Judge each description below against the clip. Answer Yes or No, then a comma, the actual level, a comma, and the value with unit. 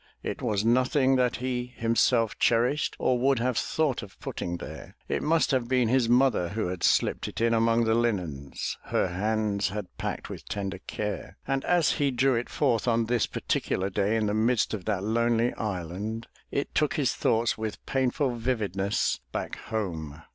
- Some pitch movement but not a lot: Yes, average, 3.6 semitones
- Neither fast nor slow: Yes, average, 180 wpm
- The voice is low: Yes, low, 115 Hz